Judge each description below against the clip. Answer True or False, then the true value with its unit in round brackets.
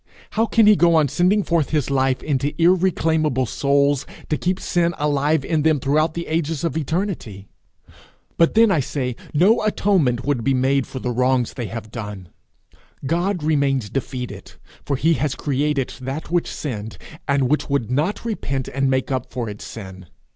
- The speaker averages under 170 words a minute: False (175 wpm)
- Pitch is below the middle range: False (145 Hz)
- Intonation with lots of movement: False (4.3 semitones)